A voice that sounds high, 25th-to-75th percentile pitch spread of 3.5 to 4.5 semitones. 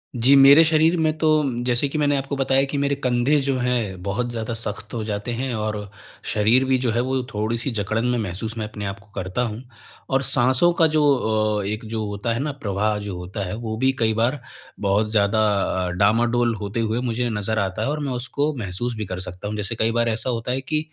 No: low, 115 Hz; average, 3.9 semitones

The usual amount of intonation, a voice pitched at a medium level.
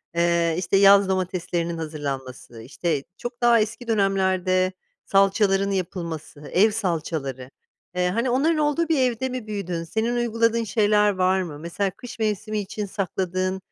No: average, 4.4 semitones; high, 195 Hz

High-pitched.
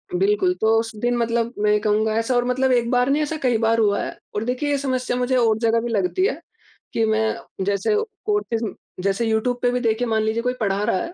Yes: high, 235 Hz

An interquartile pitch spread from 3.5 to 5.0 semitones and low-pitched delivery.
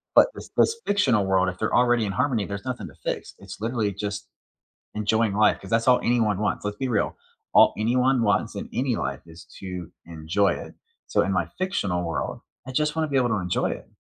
Yes: average, 4.2 semitones; low, 110 Hz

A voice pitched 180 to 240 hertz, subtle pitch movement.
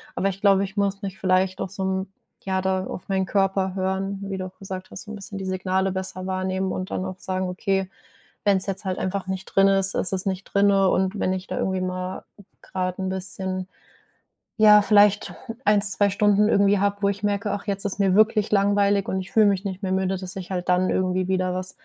Yes: high, 190 Hz; narrow, 1.1 semitones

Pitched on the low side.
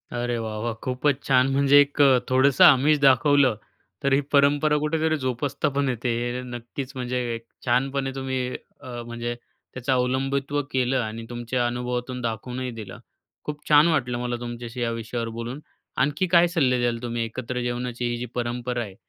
Yes: low, 125 Hz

